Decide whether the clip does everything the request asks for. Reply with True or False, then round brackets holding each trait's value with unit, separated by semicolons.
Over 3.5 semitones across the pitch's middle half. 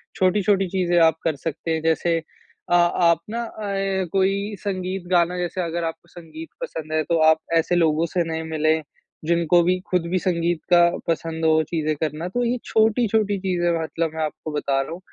False (2.5 semitones)